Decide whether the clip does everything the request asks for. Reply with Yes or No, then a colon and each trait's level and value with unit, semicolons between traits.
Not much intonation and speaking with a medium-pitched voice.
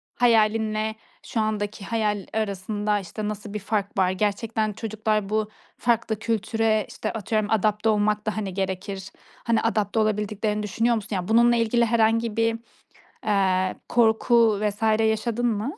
No: narrow, 1.4 semitones; high, 215 Hz